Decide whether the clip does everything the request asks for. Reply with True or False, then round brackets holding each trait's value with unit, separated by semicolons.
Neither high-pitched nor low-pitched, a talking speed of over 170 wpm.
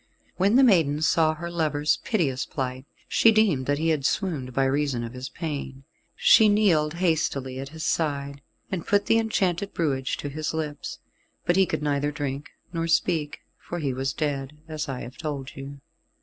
True (150 Hz; 180 wpm)